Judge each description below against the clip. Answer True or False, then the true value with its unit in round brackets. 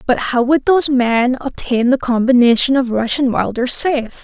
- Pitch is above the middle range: True (255 Hz)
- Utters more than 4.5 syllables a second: True (4.9 syllables/s)